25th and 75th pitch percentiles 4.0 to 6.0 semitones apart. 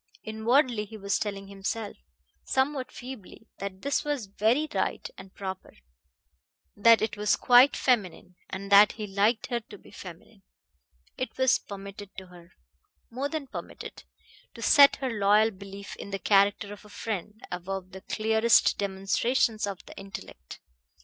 No: average, 3.2 semitones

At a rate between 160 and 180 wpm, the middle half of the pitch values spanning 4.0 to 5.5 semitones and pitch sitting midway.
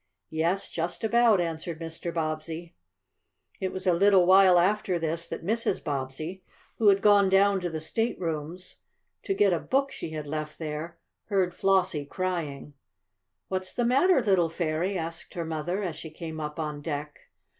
No: average, 165 wpm; average, 3.4 semitones; medium, 170 Hz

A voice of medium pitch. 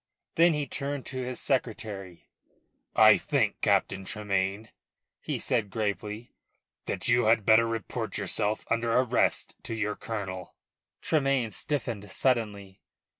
No: low, 110 Hz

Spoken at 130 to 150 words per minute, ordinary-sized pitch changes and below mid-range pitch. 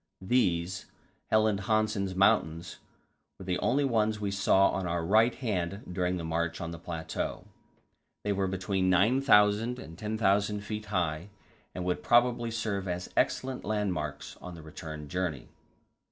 Yes: average, 145 wpm; average, 3.9 semitones; very low, 95 Hz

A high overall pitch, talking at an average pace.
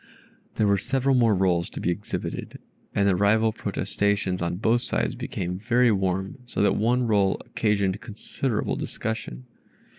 No: low, 100 Hz; average, 150 wpm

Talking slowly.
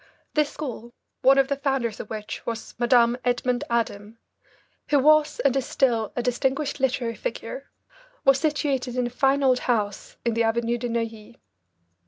No: average, 165 wpm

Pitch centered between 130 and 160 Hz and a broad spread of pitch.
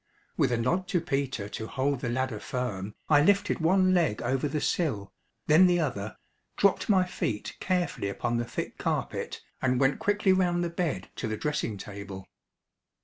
Yes: low, 135 Hz; wide, 7.7 semitones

